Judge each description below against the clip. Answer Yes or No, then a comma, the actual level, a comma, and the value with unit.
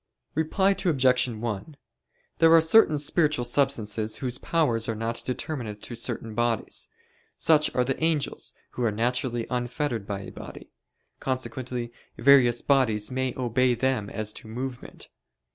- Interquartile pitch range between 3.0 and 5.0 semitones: Yes, average, 3.6 semitones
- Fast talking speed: No, average, 140 wpm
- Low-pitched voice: Yes, low, 125 Hz